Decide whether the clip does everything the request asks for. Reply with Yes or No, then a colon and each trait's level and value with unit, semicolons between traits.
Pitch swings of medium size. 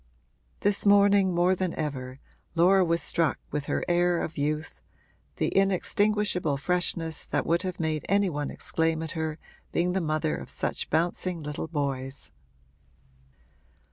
Yes: average, 3.3 semitones